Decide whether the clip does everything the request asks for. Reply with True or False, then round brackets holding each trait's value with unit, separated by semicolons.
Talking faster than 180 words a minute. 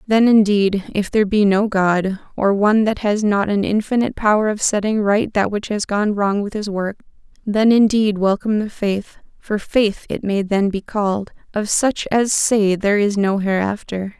True (195 wpm)